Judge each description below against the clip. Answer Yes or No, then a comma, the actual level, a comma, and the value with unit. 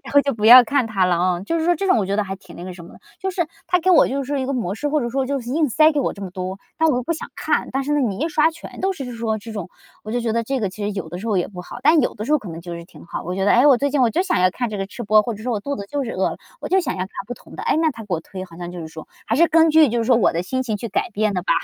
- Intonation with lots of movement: Yes, wide, 6.7 semitones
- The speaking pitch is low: No, high, 235 Hz